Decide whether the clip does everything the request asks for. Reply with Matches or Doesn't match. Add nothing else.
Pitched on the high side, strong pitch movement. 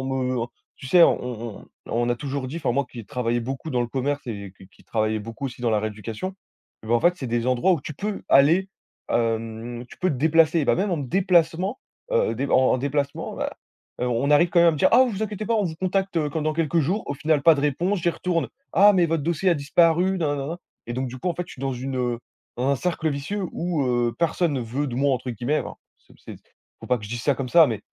Doesn't match